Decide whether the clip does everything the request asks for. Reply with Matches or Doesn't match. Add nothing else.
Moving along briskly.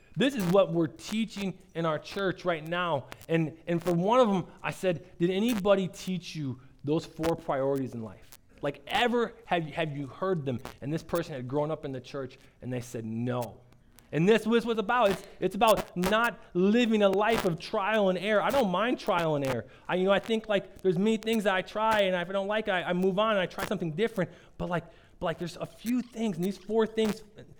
Matches